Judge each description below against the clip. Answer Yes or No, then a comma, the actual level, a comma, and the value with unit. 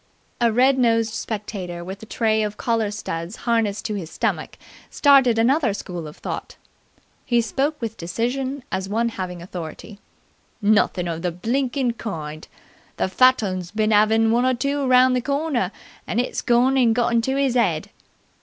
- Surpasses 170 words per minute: No, average, 165 wpm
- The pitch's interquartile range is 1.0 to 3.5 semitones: No, average, 4.5 semitones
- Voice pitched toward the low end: No, high, 225 Hz